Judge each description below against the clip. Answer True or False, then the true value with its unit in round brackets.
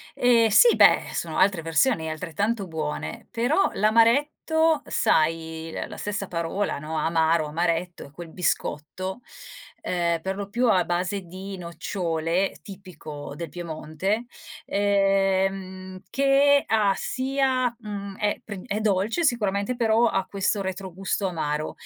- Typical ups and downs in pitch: True (4.5 semitones)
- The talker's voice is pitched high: True (195 Hz)